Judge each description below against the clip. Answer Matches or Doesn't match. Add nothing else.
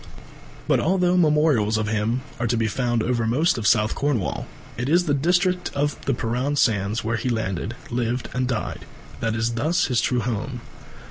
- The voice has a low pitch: Matches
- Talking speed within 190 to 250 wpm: Doesn't match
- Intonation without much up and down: Doesn't match